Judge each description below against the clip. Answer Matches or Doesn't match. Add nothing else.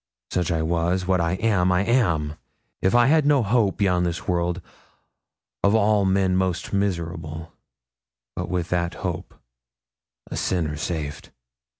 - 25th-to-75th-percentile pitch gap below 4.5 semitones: Matches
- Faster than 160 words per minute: Doesn't match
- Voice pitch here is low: Matches